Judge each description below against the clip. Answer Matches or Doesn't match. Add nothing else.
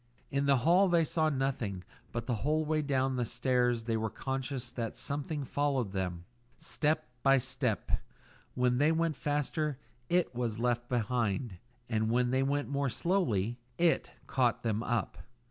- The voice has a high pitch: Doesn't match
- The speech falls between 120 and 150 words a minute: Doesn't match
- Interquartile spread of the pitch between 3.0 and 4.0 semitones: Matches